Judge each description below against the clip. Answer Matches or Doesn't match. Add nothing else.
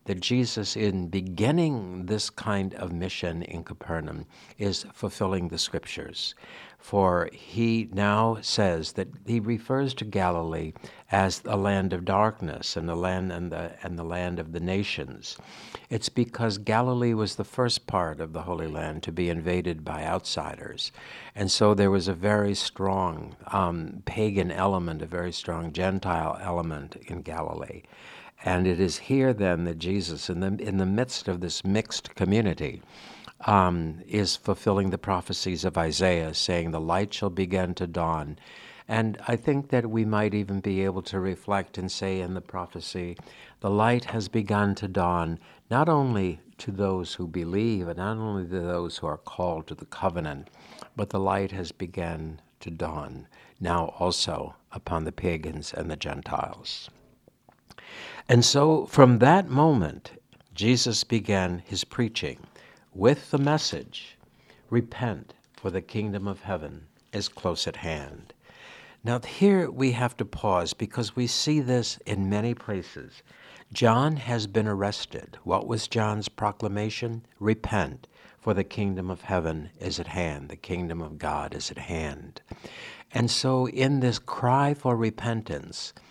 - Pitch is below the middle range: Matches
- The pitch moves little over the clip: Doesn't match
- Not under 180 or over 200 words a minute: Doesn't match